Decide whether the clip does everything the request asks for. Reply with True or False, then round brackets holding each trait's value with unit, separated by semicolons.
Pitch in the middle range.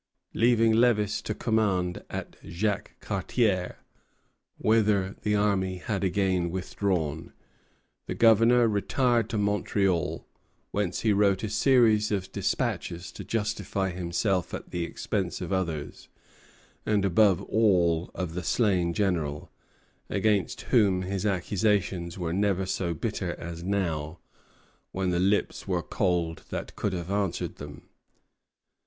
False (95 Hz)